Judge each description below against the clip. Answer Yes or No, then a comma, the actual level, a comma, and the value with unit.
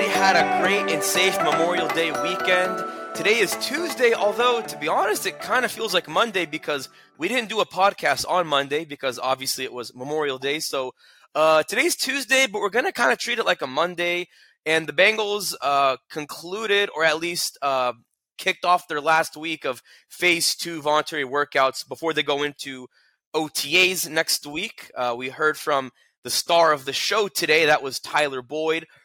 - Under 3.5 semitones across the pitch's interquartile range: No, average, 5.0 semitones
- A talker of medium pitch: Yes, medium, 160 Hz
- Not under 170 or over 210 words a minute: Yes, average, 185 wpm